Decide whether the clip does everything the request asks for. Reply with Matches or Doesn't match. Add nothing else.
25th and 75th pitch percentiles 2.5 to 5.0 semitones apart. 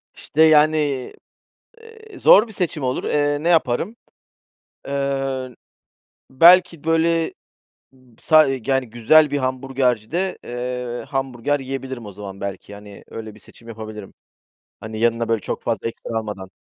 Doesn't match